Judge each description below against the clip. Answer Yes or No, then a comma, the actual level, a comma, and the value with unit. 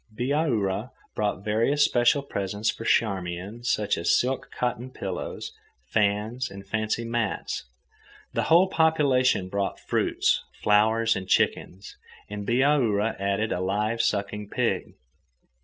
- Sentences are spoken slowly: Yes, slow, 120 wpm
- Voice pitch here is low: Yes, low, 110 Hz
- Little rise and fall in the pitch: No, average, 3.7 semitones